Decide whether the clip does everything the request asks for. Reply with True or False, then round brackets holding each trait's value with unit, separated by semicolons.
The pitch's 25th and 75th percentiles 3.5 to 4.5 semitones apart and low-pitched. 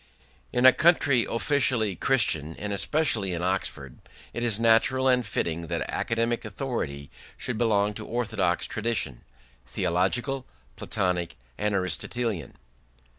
False (5.2 semitones; 110 Hz)